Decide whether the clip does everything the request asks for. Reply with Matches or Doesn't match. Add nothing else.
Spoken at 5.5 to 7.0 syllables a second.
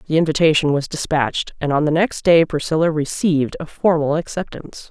Matches